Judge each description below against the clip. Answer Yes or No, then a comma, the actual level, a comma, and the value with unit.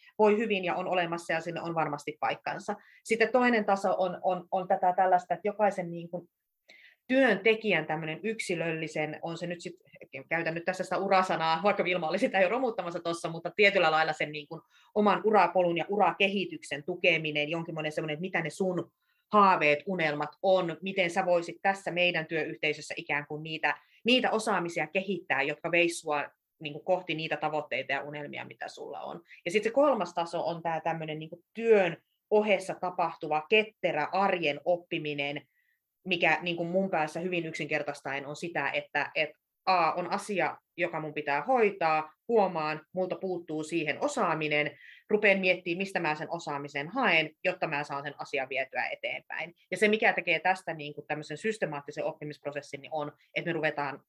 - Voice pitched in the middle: Yes, medium, 170 Hz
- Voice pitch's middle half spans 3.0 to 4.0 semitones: Yes, average, 3.7 semitones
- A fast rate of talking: Yes, fast, 160 wpm